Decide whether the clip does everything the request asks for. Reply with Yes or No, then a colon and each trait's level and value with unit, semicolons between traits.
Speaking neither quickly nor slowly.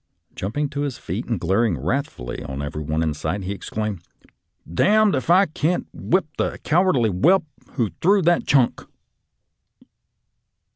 Yes: average, 160 wpm